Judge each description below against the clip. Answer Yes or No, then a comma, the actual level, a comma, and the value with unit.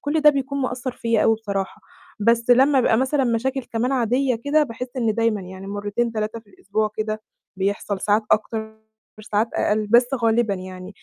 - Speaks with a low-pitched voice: No, high, 225 Hz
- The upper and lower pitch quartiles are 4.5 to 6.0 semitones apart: No, average, 3.2 semitones